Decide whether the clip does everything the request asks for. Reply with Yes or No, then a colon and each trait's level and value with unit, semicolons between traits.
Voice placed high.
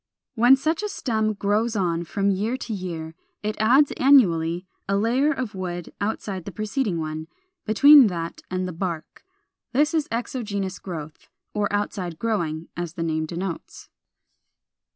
Yes: high, 200 Hz